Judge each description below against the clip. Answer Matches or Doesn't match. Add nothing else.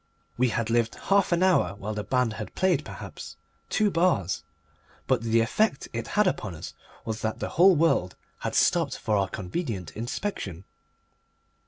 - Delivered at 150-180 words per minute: Matches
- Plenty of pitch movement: Matches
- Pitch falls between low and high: Doesn't match